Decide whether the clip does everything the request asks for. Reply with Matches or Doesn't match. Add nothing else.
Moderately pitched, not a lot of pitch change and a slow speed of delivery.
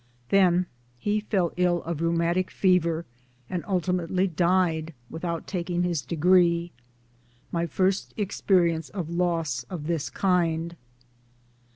Matches